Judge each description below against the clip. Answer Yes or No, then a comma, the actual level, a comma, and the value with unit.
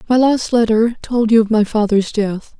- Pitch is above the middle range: Yes, high, 225 Hz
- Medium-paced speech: No, fast, 210 wpm